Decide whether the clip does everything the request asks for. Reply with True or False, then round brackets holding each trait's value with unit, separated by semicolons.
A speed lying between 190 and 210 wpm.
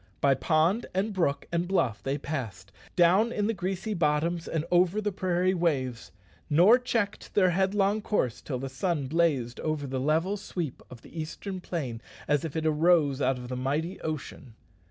False (175 wpm)